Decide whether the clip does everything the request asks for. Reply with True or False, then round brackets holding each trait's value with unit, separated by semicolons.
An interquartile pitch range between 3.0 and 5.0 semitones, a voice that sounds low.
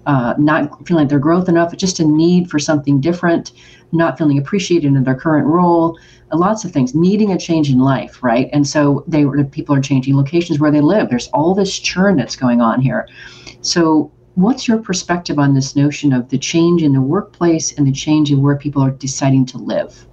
False (3.8 semitones; 150 Hz)